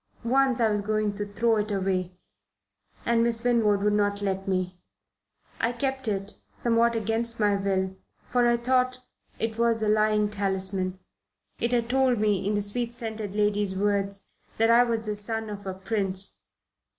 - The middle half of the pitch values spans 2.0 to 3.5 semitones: Yes, average, 2.7 semitones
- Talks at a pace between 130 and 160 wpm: No, average, 170 wpm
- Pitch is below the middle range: No, high, 210 Hz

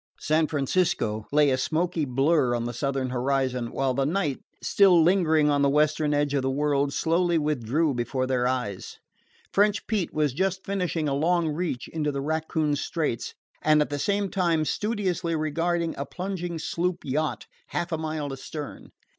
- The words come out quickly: No, average, 170 wpm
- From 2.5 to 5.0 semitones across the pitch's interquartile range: Yes, average, 3.8 semitones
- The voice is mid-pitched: Yes, medium, 155 Hz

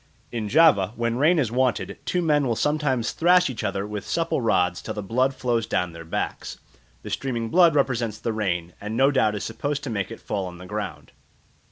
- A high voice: No, low, 115 Hz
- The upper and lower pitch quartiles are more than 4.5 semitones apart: Yes, average, 5.2 semitones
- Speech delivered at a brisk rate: Yes, fast, 210 wpm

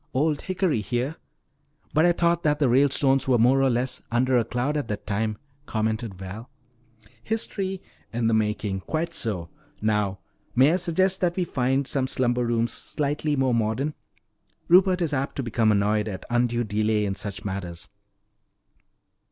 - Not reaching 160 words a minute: No, average, 165 wpm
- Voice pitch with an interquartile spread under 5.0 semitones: No, wide, 5.5 semitones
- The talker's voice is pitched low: Yes, low, 125 Hz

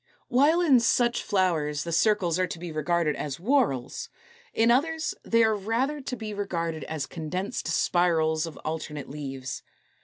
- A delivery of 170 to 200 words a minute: No, average, 155 wpm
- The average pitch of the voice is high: No, medium, 180 Hz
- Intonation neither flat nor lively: No, wide, 6.6 semitones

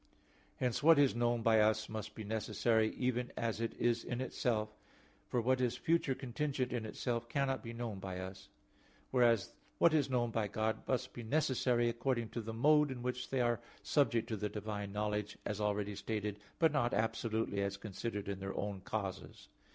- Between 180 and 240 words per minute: Yes, average, 185 wpm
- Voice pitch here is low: Yes, low, 115 Hz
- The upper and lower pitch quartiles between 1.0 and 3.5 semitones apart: Yes, average, 3.0 semitones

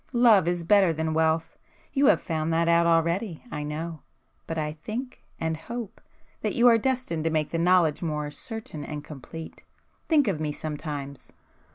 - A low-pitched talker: No, medium, 165 Hz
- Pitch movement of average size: Yes, average, 4.7 semitones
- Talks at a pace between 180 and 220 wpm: No, average, 155 wpm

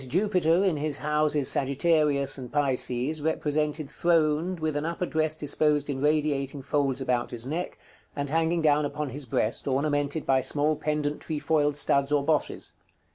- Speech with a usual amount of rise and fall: No, narrow, 2.0 semitones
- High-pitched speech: No, medium, 150 Hz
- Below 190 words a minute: Yes, average, 160 wpm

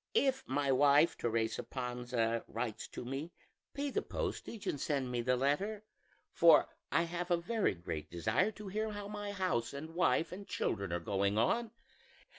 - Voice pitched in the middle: Yes, medium, 145 Hz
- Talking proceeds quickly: No, average, 170 wpm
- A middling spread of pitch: No, wide, 9.0 semitones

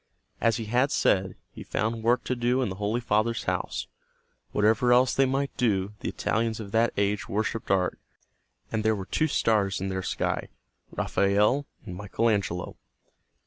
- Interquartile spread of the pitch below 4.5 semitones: Yes, average, 3.3 semitones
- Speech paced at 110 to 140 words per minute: No, average, 170 wpm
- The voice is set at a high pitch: No, low, 110 Hz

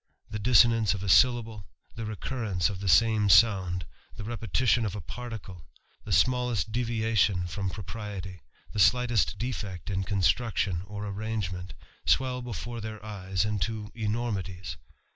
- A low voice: Yes, low, 105 Hz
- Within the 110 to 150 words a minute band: Yes, average, 140 wpm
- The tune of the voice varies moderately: Yes, average, 3.3 semitones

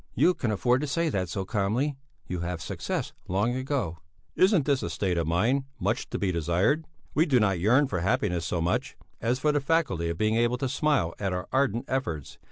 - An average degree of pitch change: No, wide, 7.3 semitones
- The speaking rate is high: Yes, fast, 215 wpm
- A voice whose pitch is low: Yes, low, 110 Hz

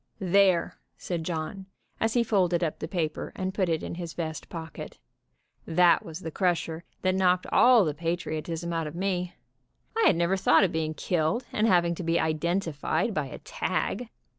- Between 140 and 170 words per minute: No, average, 180 wpm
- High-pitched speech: No, medium, 170 Hz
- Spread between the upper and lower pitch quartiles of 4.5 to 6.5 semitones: No, average, 2.7 semitones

